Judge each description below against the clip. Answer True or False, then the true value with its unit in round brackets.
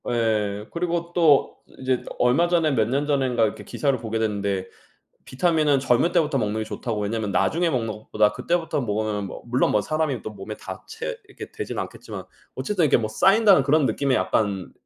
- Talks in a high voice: False (125 Hz)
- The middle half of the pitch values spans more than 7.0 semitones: False (6.7 semitones)